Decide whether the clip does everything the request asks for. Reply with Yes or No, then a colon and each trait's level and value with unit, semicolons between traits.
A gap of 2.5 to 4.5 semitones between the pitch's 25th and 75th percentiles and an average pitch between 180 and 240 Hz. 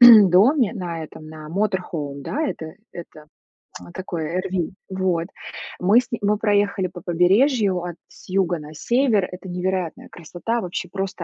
Yes: average, 3.3 semitones; medium, 185 Hz